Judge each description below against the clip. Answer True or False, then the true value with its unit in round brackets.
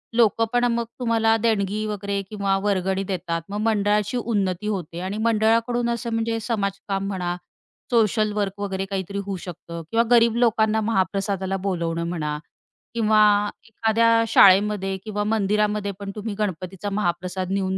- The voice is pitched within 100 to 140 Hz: False (205 Hz)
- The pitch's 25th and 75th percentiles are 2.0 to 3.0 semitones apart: True (2.6 semitones)